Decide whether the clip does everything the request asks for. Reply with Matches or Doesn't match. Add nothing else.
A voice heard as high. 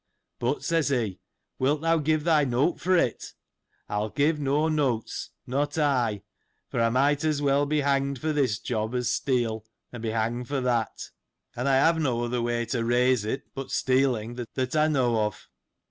Doesn't match